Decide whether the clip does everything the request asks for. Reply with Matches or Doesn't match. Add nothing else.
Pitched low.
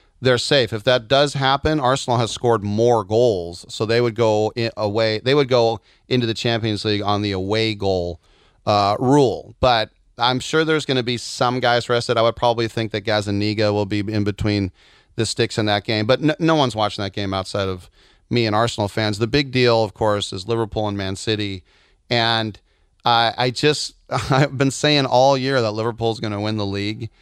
Matches